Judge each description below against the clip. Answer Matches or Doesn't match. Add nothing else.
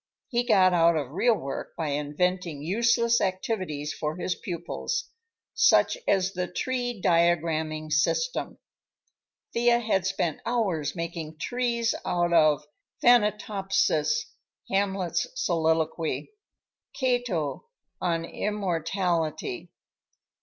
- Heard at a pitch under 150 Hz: Doesn't match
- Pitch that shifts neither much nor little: Doesn't match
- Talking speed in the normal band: Doesn't match